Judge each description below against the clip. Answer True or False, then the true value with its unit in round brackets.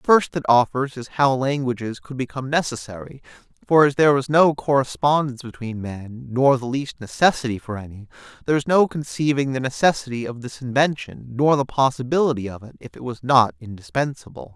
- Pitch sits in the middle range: False (130 Hz)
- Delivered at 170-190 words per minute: True (175 wpm)